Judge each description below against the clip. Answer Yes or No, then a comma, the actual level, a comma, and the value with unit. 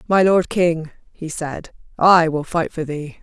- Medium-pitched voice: Yes, medium, 165 Hz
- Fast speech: No, average, 185 wpm